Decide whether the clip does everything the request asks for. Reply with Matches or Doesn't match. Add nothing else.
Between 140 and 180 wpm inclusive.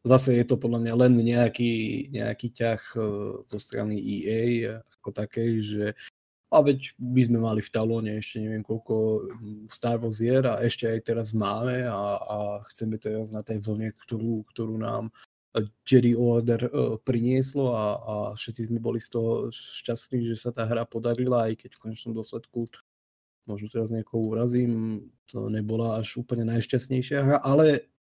Matches